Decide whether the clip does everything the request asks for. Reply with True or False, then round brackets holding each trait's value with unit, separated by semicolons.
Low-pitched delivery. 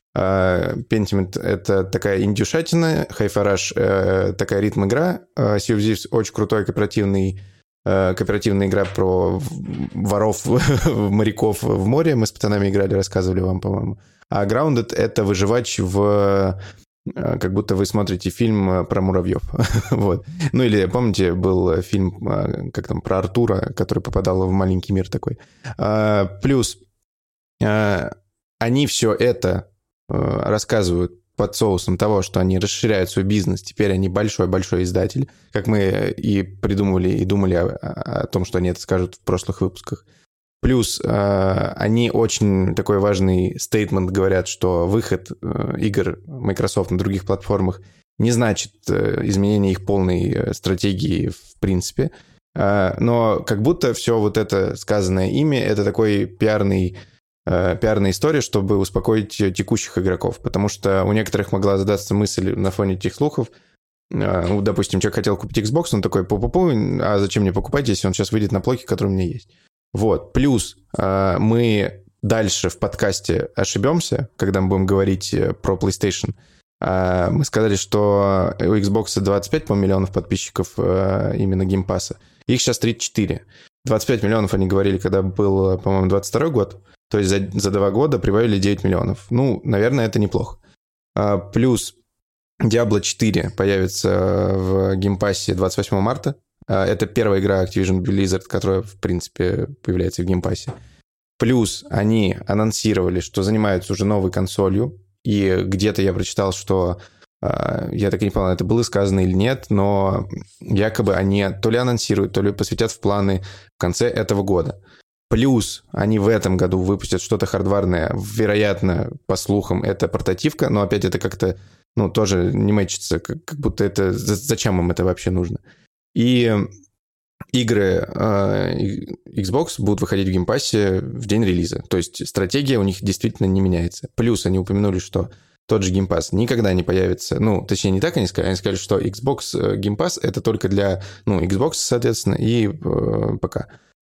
True (100 Hz)